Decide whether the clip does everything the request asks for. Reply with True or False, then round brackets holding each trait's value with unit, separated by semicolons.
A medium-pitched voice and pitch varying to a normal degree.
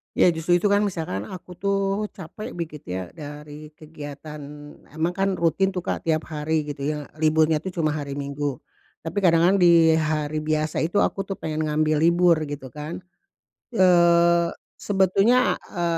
True (160 Hz; 3.0 semitones)